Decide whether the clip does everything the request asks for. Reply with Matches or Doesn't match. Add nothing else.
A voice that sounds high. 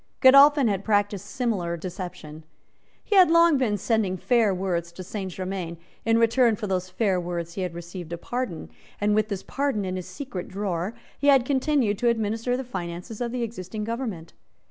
Matches